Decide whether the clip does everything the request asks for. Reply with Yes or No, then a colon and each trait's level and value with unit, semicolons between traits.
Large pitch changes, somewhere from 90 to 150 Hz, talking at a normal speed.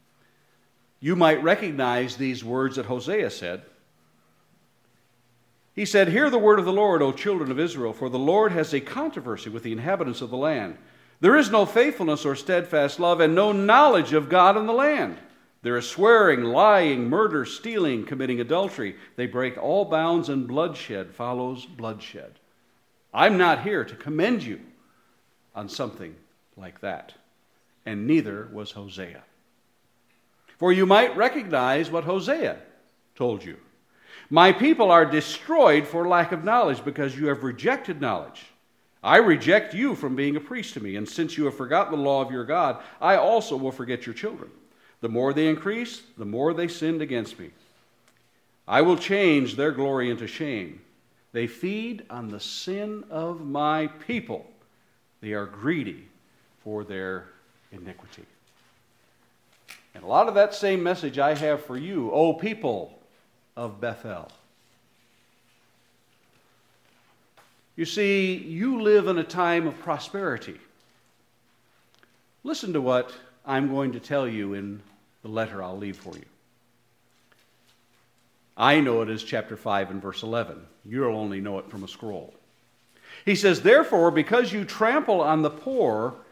Yes: wide, 7.3 semitones; medium, 140 Hz; average, 150 wpm